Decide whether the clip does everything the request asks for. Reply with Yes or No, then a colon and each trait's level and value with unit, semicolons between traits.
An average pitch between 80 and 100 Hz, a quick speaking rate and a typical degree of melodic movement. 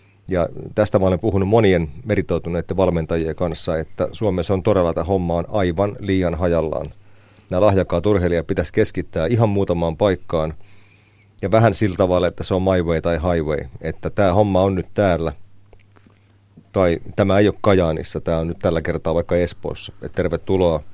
Yes: very low, 95 Hz; fast, 165 wpm; average, 3.2 semitones